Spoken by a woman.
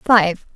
Yes: female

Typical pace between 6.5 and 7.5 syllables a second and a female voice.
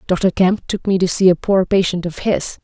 No: 4.9 syllables/s; female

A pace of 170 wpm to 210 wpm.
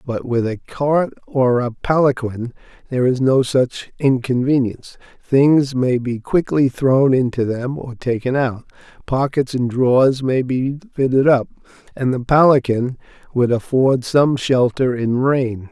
No: average, 145 wpm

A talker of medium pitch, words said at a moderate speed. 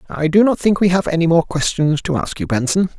No: medium, 165 Hz; fast, 260 wpm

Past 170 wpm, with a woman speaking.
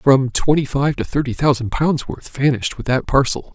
No: fast, 205 wpm; male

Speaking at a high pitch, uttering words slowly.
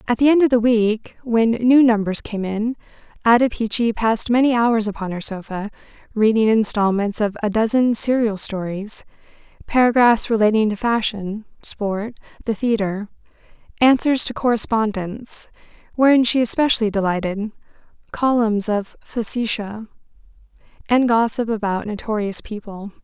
Yes: high, 220 Hz; slow, 125 wpm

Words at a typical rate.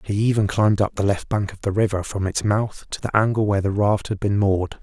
No: fast, 275 wpm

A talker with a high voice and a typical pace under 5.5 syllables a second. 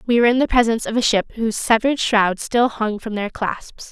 No: high, 225 Hz; 5.9 syllables/s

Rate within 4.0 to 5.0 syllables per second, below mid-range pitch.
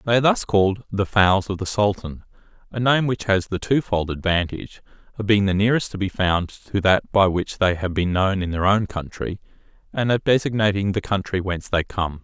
No: 5.4 syllables/s; low, 100 Hz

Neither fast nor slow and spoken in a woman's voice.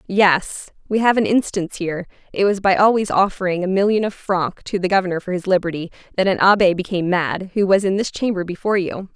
No: fast, 215 wpm; female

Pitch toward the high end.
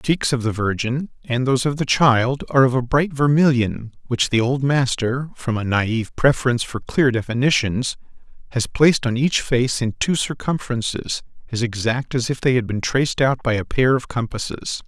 No: low, 125 Hz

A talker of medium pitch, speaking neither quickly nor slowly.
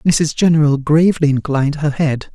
Yes: medium, 150 Hz; average, 155 wpm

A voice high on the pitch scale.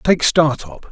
No: medium, 140 Hz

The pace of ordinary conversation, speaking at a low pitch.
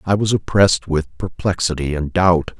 Yes: average, 160 wpm; very low, 90 Hz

